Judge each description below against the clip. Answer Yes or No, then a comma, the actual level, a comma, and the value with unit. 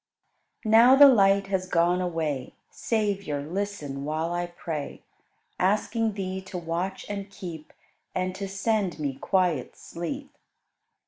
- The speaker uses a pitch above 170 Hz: Yes, medium, 185 Hz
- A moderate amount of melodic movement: Yes, average, 3.4 semitones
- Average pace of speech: No, slow, 130 wpm